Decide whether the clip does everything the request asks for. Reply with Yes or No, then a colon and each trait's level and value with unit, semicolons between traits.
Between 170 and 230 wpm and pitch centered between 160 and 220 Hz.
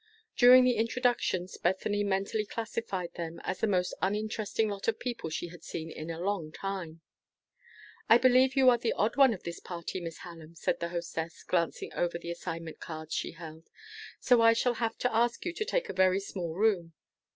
Yes: average, 195 wpm; high, 190 Hz